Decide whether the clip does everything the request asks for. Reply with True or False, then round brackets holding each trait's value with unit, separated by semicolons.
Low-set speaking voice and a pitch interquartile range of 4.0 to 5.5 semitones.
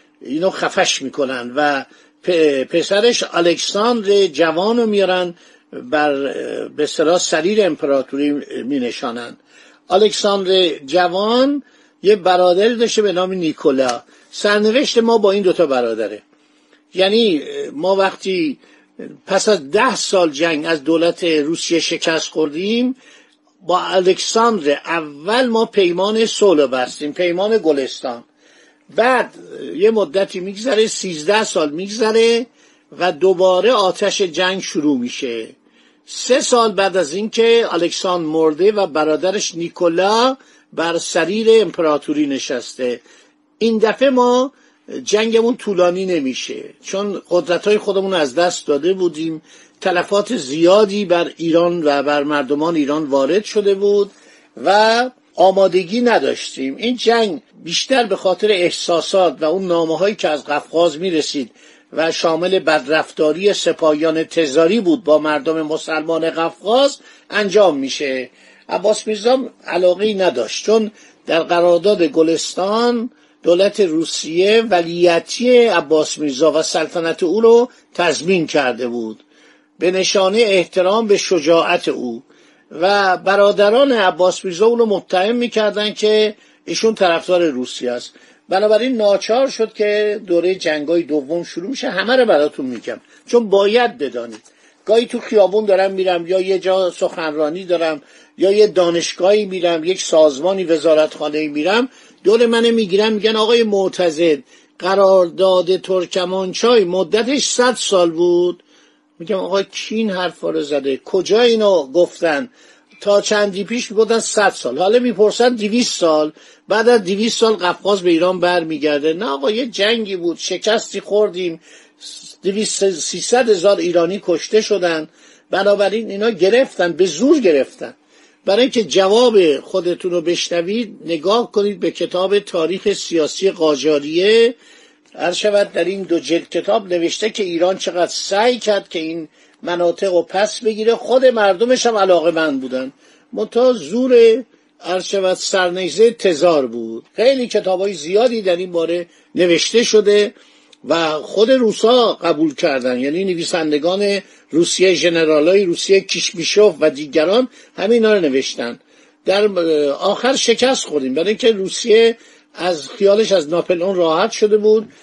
False (190 Hz; 4.7 semitones)